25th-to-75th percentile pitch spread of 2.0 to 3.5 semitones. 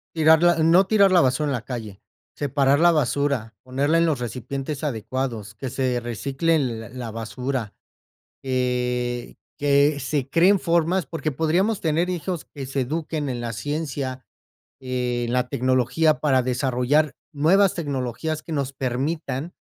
No: average, 4.1 semitones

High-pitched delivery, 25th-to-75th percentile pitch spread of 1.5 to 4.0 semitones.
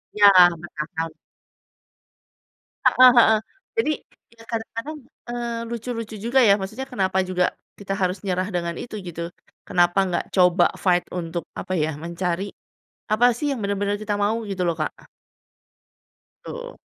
No: high, 200 Hz; average, 4.4 semitones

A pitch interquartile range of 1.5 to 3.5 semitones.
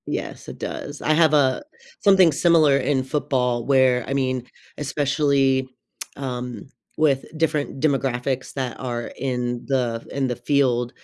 Yes: narrow, 2.6 semitones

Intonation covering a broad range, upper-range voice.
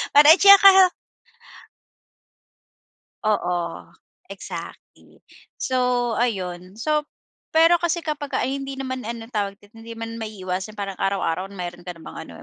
Yes: wide, 6.5 semitones; high, 230 Hz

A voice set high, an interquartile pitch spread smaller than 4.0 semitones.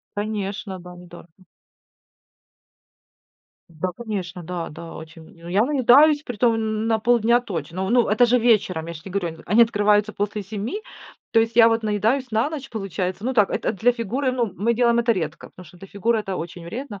No: high, 215 Hz; average, 4.4 semitones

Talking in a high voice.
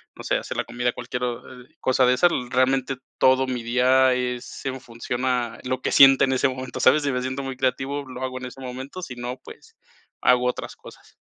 No: low, 130 Hz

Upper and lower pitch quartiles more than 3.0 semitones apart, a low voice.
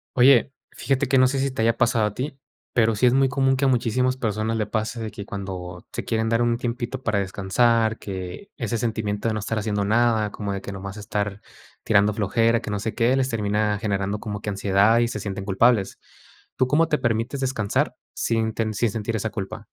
No: average, 2.7 semitones; low, 110 Hz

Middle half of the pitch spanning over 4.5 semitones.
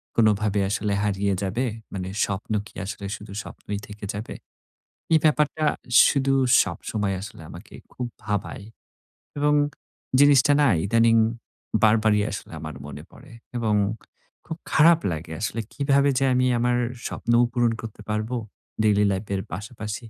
No: average, 3.7 semitones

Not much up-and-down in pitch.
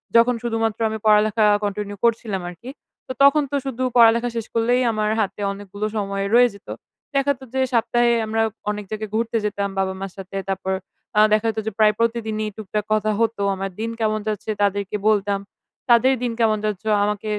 Yes: narrow, 2.2 semitones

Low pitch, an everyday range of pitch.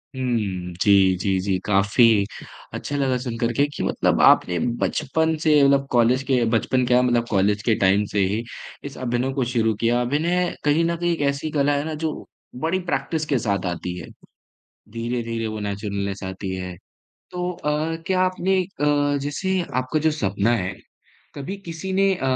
No: low, 125 Hz; wide, 6.5 semitones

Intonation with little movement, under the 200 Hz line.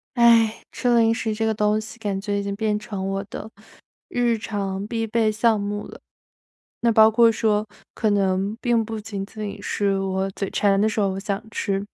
No: narrow, 2.0 semitones; high, 210 Hz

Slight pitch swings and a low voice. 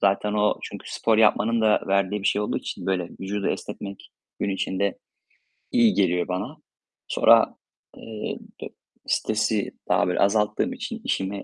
Yes: narrow, 1.7 semitones; low, 100 Hz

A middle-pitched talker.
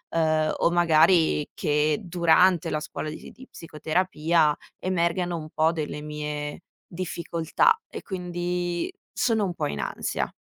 Yes: medium, 165 Hz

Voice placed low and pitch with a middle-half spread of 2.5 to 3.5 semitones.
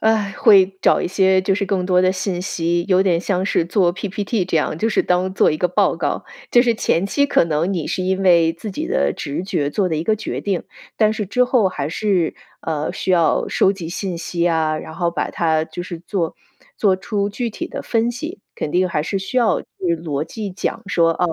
No: medium, 185 Hz; average, 3.2 semitones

